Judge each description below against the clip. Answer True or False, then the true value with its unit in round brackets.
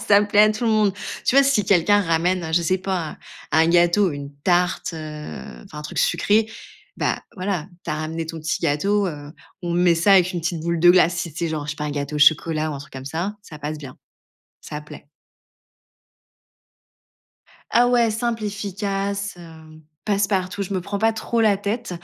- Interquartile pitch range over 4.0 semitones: True (4.4 semitones)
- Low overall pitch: False (175 Hz)